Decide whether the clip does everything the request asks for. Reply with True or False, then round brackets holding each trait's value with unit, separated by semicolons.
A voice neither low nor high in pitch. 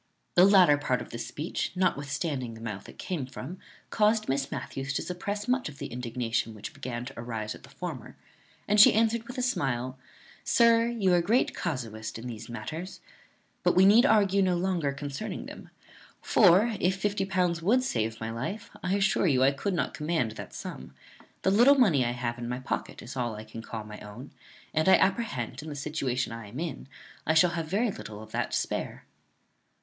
True (150 Hz)